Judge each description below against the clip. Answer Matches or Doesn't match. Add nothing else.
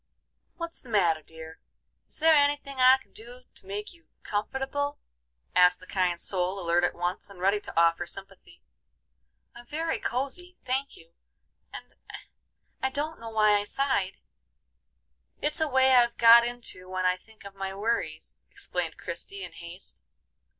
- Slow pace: Doesn't match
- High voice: Matches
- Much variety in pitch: Matches